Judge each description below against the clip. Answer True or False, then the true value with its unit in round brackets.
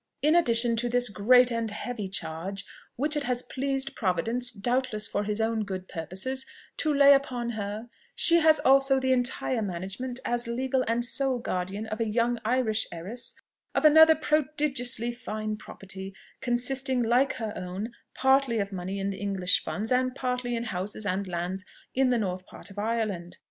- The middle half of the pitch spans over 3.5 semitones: True (4.4 semitones)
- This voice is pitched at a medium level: False (235 Hz)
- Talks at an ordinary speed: True (170 wpm)